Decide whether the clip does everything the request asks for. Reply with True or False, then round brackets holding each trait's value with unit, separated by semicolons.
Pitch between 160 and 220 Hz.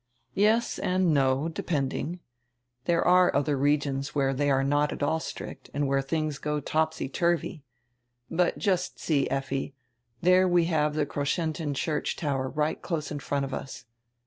False (150 Hz)